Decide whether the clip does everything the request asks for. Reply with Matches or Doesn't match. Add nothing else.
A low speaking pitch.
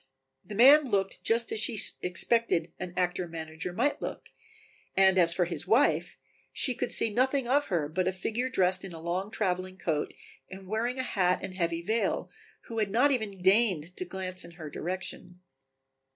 Doesn't match